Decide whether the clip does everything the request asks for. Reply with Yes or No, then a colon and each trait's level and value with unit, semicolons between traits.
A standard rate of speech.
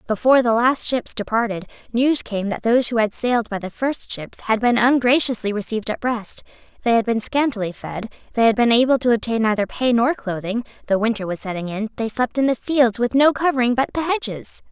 No: fast, 215 wpm